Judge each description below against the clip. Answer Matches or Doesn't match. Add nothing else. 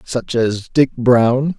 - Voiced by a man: Matches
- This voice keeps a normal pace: Matches